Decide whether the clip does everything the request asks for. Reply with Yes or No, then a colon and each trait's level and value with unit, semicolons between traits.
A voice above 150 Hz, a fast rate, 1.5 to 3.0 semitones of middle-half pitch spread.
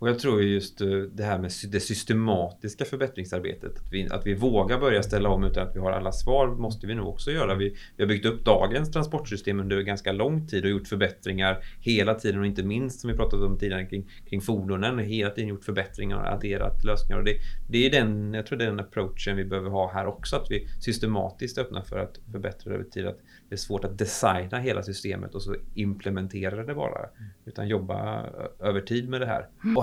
No: low, 100 Hz; fast, 220 wpm; narrow, 2.5 semitones